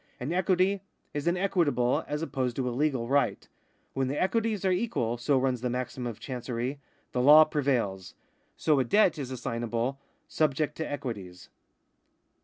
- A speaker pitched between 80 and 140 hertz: Yes, low, 135 Hz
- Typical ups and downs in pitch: Yes, average, 4.2 semitones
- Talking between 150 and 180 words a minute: Yes, average, 175 wpm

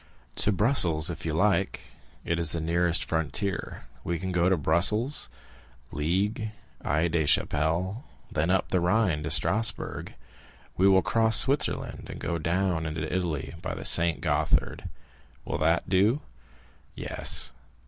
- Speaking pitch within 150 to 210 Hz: No, very low, 85 Hz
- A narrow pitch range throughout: No, average, 3.5 semitones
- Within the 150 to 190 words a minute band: No, average, 140 wpm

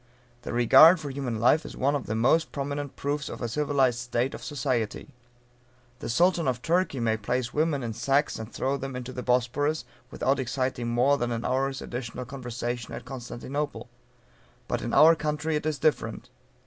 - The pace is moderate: Yes, average, 180 wpm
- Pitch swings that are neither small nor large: Yes, average, 3.1 semitones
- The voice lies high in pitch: No, low, 130 Hz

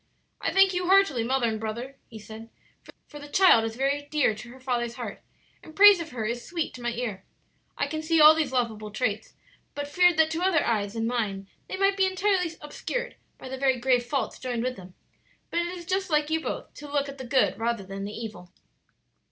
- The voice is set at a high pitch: Yes, very high, 265 Hz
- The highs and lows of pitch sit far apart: Yes, wide, 6.0 semitones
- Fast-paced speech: Yes, fast, 225 wpm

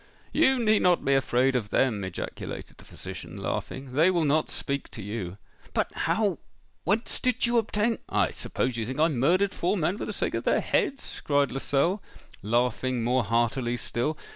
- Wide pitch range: Yes, wide, 7.6 semitones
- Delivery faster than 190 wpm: No, average, 175 wpm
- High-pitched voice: No, medium, 140 Hz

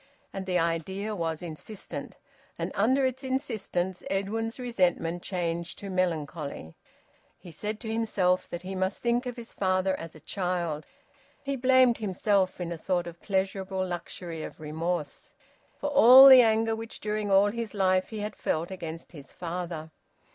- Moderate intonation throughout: Yes, average, 4.4 semitones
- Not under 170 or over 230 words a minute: No, average, 160 wpm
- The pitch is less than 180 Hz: No, high, 190 Hz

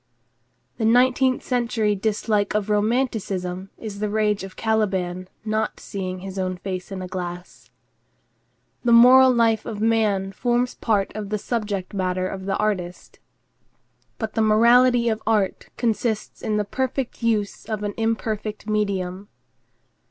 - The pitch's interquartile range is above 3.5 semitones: No, average, 2.9 semitones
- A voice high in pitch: Yes, high, 210 Hz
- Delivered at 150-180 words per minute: No, average, 140 wpm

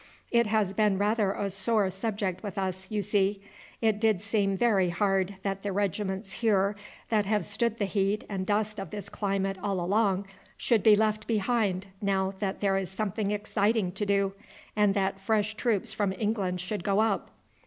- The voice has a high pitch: Yes, high, 200 Hz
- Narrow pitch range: Yes, narrow, 1.8 semitones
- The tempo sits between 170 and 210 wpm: Yes, average, 180 wpm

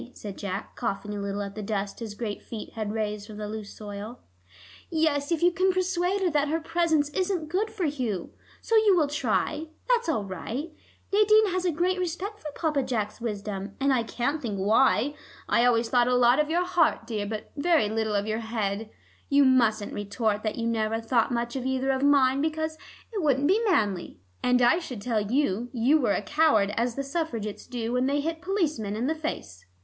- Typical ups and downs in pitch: No, wide, 6.7 semitones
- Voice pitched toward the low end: No, very high, 250 Hz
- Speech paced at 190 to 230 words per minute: Yes, fast, 205 wpm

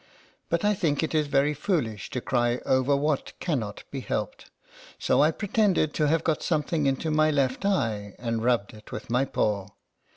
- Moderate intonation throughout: Yes, average, 4.6 semitones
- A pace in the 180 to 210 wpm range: Yes, average, 190 wpm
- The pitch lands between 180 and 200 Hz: No, medium, 140 Hz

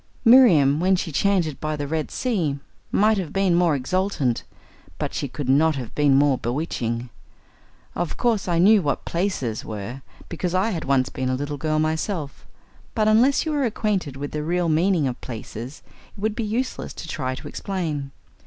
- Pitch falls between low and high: Yes, medium, 160 Hz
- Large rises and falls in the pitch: Yes, wide, 6.0 semitones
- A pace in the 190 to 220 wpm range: No, average, 180 wpm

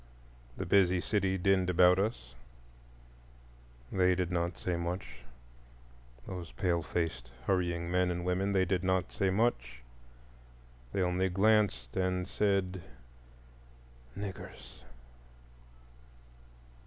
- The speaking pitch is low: Yes, very low, 90 Hz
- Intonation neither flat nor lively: No, narrow, 2.0 semitones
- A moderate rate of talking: No, slow, 100 wpm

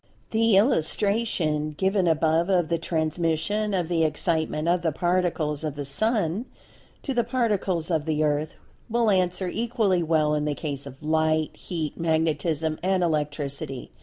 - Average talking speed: Yes, average, 150 wpm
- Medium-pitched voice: Yes, medium, 165 Hz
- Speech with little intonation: No, average, 3.7 semitones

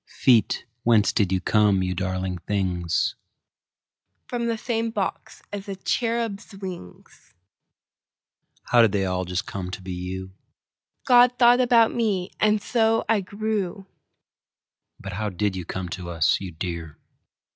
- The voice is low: Yes, low, 105 Hz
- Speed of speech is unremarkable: No, slow, 130 wpm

